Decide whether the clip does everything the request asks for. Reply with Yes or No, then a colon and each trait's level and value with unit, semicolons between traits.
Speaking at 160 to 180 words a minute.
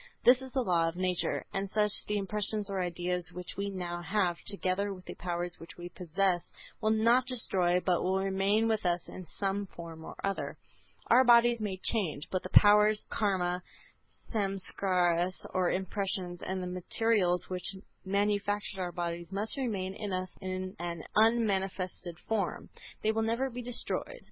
Yes: average, 170 wpm